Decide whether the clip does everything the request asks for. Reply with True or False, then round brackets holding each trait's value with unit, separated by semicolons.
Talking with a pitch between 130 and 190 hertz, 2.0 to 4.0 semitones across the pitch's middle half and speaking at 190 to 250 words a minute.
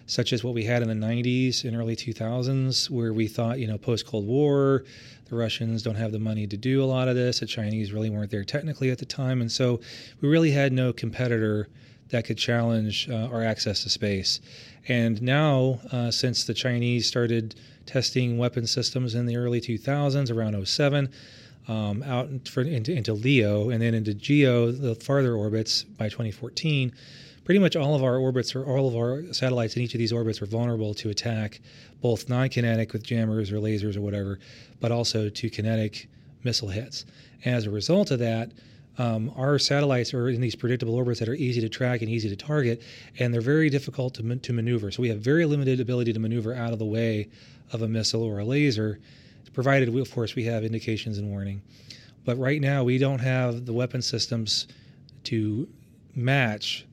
False (120 Hz; 2.4 semitones; 195 wpm)